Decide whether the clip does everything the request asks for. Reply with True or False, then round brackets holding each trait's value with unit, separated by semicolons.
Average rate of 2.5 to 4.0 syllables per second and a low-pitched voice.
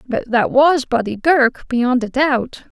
False (3.7 syllables/s; 255 Hz)